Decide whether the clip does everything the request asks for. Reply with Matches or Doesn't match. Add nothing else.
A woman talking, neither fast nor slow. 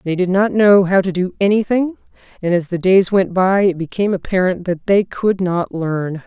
Doesn't match